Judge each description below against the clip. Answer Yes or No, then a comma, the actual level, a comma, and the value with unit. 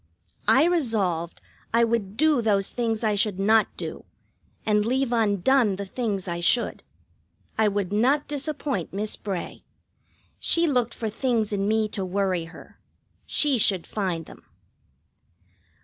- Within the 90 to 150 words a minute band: Yes, average, 140 wpm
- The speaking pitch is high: Yes, high, 215 Hz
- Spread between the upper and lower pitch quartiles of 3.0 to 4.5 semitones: Yes, average, 3.8 semitones